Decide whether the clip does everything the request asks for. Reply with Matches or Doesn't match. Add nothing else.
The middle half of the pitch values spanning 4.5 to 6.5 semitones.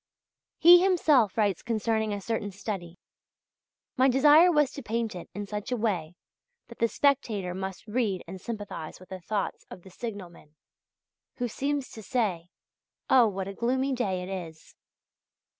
Matches